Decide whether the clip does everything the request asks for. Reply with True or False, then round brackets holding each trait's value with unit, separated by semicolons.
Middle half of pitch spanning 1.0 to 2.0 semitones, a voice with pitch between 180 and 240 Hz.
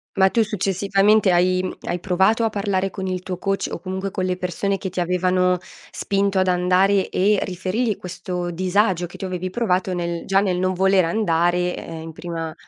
True (1.6 semitones; 185 Hz)